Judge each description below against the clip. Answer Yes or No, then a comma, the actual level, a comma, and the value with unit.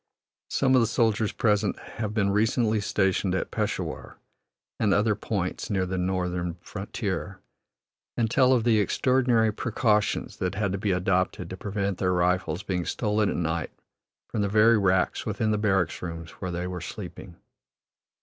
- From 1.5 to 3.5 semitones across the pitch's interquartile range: Yes, average, 3.1 semitones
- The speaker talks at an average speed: Yes, average, 160 wpm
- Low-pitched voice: Yes, low, 100 Hz